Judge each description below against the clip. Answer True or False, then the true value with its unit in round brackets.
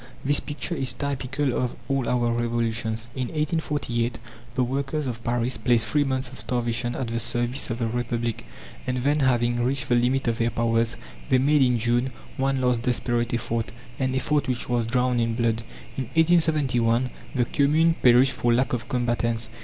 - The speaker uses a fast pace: False (175 wpm)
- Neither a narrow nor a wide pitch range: False (2.2 semitones)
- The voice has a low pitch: True (125 Hz)